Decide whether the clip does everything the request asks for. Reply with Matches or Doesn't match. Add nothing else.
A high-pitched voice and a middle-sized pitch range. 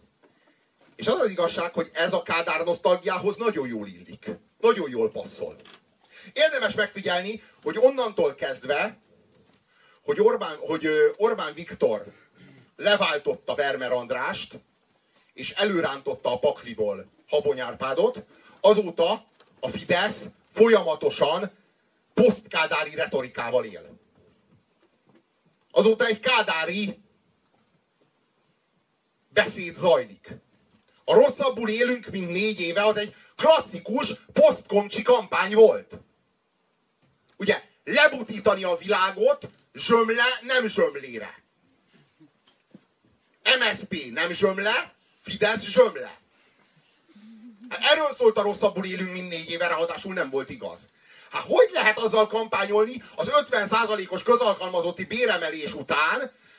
Doesn't match